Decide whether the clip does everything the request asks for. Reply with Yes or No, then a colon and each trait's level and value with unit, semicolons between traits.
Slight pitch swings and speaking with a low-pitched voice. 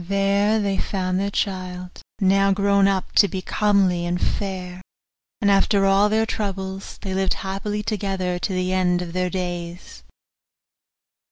No: narrow, 1.5 semitones; high, 195 Hz